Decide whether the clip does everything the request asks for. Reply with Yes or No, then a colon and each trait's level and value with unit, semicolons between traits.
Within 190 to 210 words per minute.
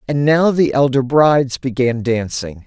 No: average, 160 wpm